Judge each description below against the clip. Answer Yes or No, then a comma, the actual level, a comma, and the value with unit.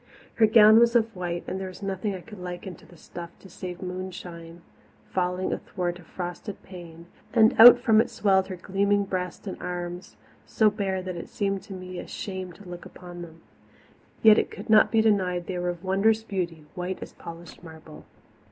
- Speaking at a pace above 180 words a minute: Yes, average, 195 wpm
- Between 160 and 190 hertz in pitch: Yes, medium, 185 Hz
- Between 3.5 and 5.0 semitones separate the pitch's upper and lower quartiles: No, narrow, 2.5 semitones